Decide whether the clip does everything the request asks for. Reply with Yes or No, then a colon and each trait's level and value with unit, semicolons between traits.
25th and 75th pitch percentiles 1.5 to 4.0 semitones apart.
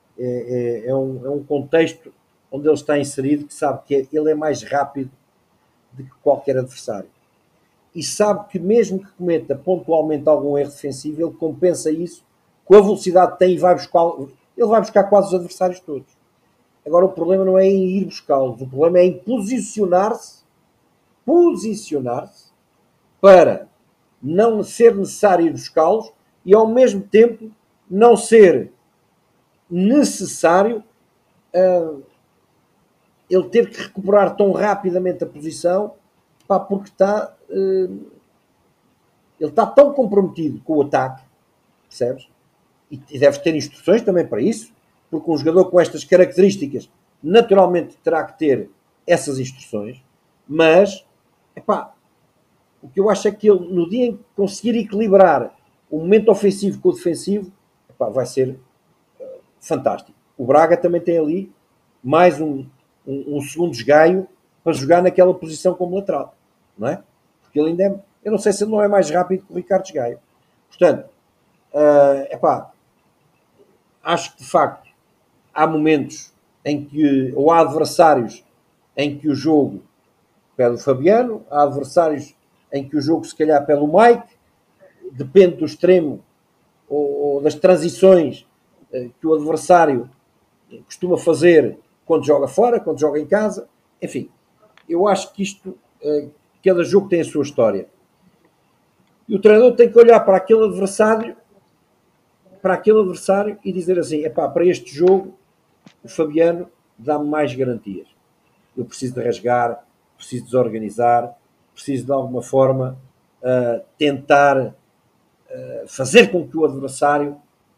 No: wide, 5.4 semitones